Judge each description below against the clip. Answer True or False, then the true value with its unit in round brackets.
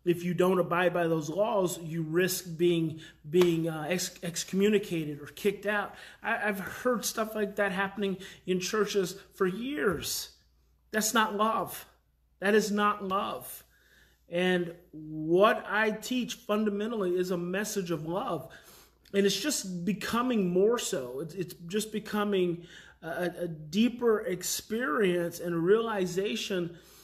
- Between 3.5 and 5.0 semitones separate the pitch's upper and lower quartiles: False (3.1 semitones)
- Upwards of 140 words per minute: False (135 wpm)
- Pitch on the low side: False (190 Hz)